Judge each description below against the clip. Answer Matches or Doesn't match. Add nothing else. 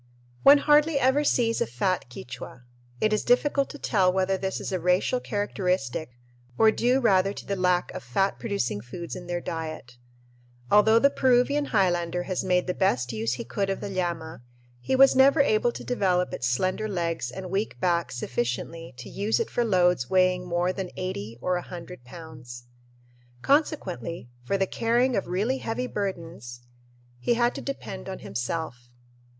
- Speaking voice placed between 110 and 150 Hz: Doesn't match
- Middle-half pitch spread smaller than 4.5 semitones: Doesn't match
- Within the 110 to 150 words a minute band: Doesn't match